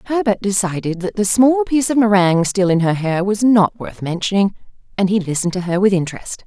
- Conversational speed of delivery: No, fast, 215 wpm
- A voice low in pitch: No, high, 200 Hz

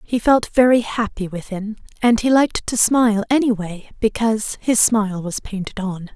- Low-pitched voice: No, high, 215 Hz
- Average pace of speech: Yes, average, 165 wpm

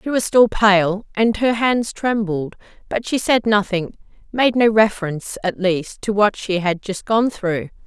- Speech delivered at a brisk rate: No, average, 185 wpm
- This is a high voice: Yes, high, 205 Hz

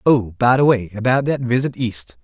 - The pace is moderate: Yes, average, 190 wpm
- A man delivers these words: Yes, male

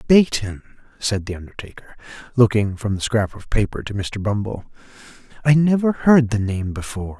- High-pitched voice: No, low, 110 Hz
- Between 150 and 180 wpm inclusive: Yes, average, 160 wpm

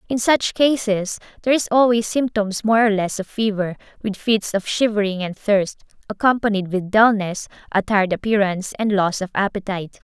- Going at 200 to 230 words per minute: No, average, 165 wpm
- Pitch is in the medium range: No, high, 210 Hz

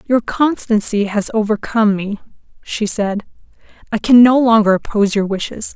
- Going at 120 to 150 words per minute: Yes, average, 145 wpm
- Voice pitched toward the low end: No, high, 215 Hz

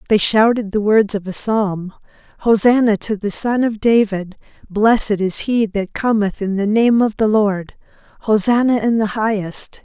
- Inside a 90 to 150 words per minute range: No, average, 170 wpm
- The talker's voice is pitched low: No, high, 215 Hz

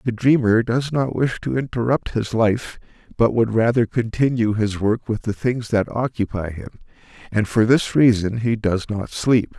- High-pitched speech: No, low, 115 Hz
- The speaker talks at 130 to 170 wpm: No, average, 180 wpm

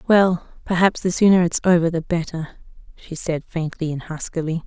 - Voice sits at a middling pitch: Yes, medium, 170 Hz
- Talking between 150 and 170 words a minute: Yes, average, 165 wpm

